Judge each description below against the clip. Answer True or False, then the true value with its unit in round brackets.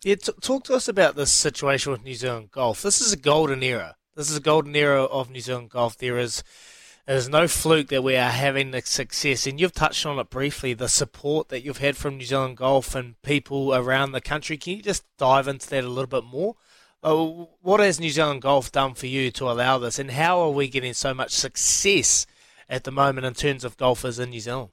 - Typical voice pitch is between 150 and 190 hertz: False (135 Hz)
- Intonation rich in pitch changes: False (2.8 semitones)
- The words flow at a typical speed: False (240 wpm)